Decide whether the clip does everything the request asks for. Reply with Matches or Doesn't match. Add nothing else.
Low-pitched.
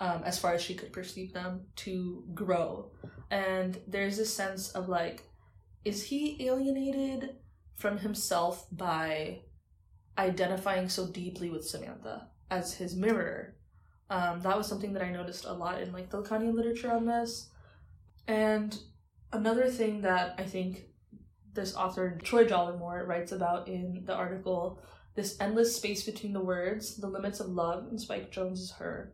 Doesn't match